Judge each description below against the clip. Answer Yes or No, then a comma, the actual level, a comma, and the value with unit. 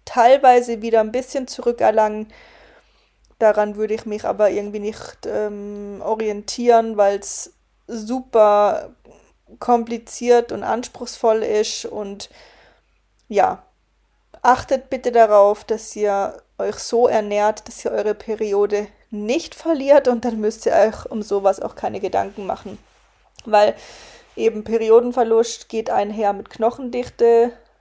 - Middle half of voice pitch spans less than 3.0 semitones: Yes, narrow, 2.4 semitones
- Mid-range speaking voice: No, high, 225 Hz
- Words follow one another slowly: Yes, slow, 120 wpm